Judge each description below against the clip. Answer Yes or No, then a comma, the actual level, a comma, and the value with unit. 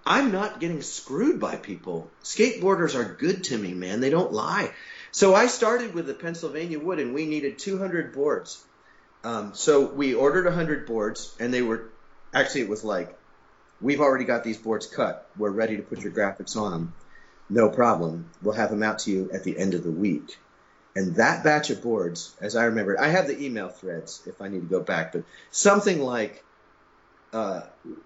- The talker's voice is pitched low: Yes, low, 130 Hz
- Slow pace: No, average, 190 wpm